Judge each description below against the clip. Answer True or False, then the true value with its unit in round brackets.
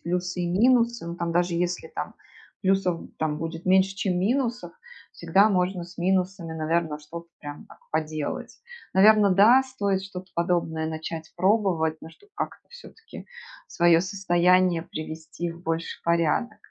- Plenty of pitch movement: False (2.9 semitones)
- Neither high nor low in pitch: True (180 Hz)